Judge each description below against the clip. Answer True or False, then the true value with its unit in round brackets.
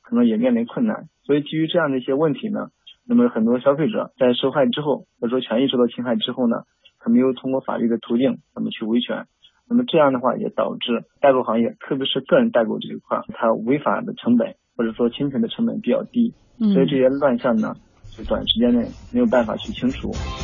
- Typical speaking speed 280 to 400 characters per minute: True (345 characters per minute)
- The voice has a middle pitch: True (160 Hz)